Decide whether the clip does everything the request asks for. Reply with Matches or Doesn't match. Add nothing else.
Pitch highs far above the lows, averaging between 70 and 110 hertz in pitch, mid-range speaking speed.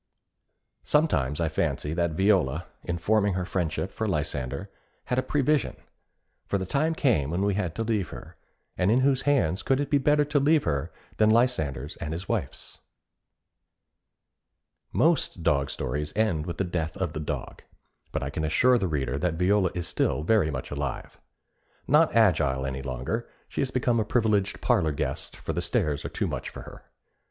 Matches